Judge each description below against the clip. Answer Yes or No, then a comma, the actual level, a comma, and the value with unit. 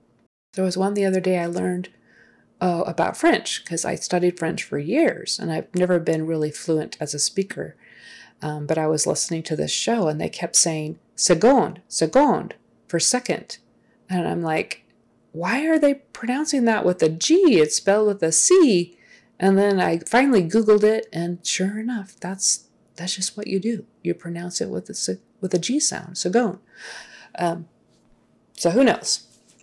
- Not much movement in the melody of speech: No, average, 4.4 semitones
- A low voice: No, medium, 180 Hz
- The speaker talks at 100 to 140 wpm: No, average, 175 wpm